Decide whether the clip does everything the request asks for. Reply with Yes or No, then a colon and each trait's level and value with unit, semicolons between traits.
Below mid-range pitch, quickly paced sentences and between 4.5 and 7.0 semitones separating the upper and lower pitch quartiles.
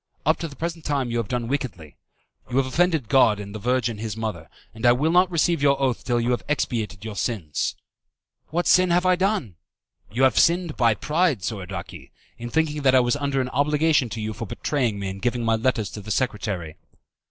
Yes: low, 125 Hz; fast, 215 wpm; wide, 5.4 semitones